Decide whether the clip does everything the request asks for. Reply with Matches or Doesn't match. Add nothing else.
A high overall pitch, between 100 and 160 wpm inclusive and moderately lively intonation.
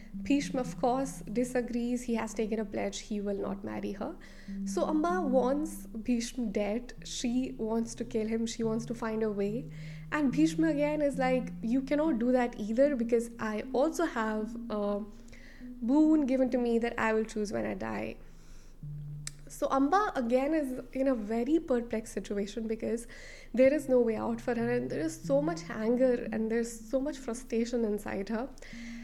Doesn't match